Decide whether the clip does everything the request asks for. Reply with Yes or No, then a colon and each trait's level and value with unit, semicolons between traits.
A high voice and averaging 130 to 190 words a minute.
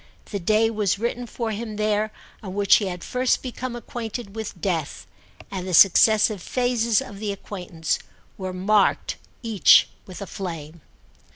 Yes: high, 210 Hz; average, 155 wpm